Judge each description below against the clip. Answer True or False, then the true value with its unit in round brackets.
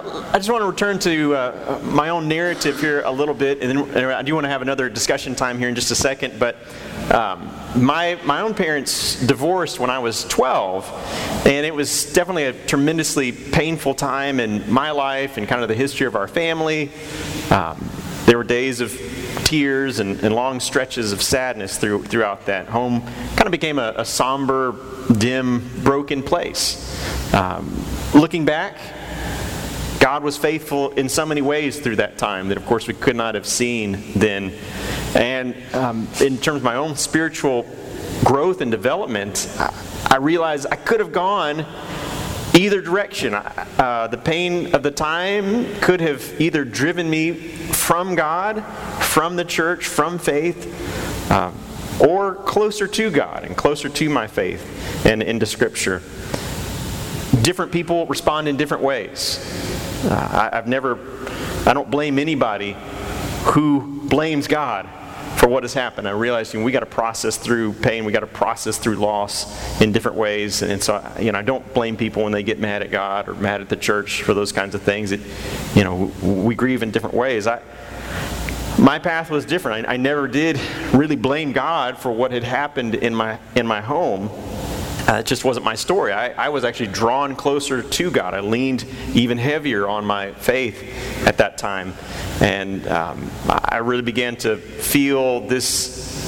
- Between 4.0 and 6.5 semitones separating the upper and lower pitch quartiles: True (4.8 semitones)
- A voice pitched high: False (130 Hz)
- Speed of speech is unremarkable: True (175 wpm)